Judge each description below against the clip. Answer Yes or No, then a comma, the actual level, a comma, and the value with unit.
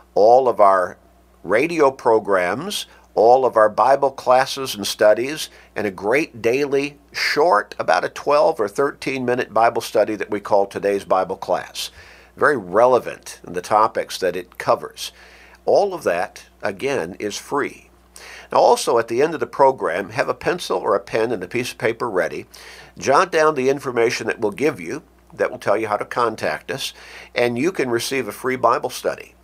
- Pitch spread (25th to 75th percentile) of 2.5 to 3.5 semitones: No, average, 4.7 semitones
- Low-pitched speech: Yes, low, 130 Hz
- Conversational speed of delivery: Yes, average, 180 wpm